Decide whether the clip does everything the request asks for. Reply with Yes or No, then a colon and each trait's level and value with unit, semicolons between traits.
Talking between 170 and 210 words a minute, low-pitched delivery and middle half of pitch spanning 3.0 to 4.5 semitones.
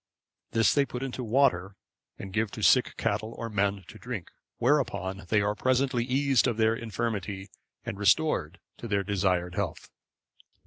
No: average, 160 wpm; low, 110 Hz; average, 4.0 semitones